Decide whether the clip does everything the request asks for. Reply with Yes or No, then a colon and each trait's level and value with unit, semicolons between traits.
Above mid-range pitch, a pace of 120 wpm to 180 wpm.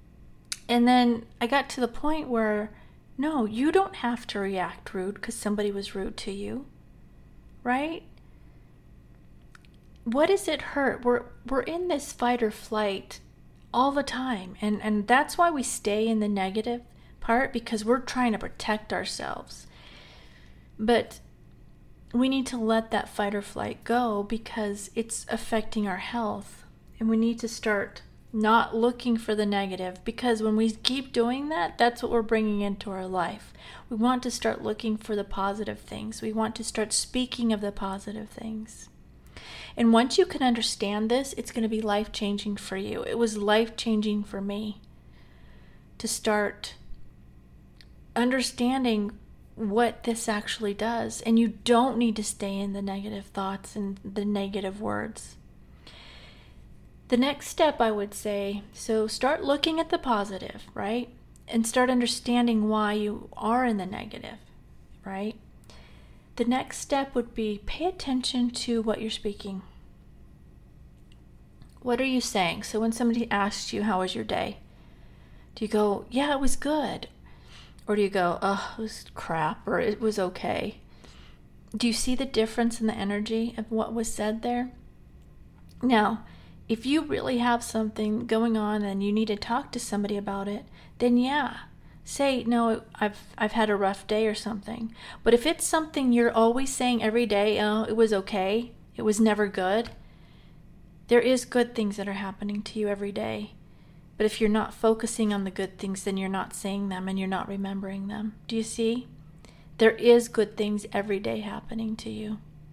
Yes: high, 220 Hz; average, 170 wpm